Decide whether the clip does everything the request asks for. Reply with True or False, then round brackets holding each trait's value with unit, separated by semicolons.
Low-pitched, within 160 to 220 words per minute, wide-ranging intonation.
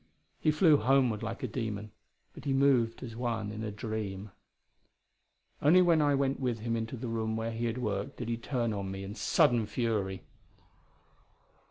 False (115 Hz; 180 wpm; 3.1 semitones)